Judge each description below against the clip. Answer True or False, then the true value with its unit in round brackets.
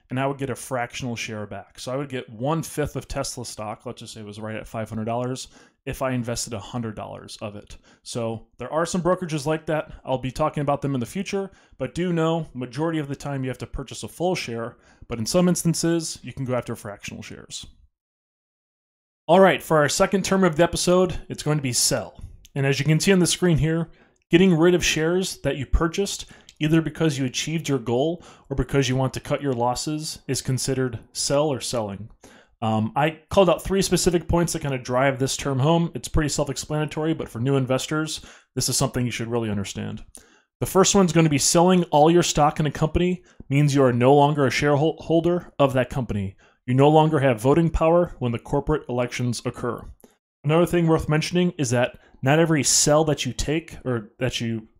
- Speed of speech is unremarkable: False (220 wpm)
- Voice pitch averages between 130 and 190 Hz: True (140 Hz)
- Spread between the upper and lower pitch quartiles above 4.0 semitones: True (4.9 semitones)